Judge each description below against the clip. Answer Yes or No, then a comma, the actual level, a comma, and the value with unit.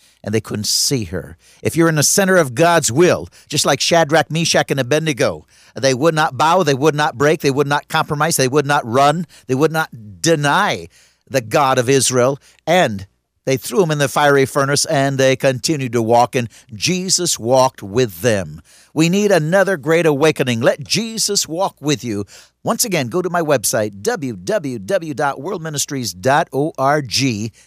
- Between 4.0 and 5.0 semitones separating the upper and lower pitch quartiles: Yes, average, 4.6 semitones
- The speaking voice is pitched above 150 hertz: No, medium, 140 Hz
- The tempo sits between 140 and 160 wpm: No, average, 170 wpm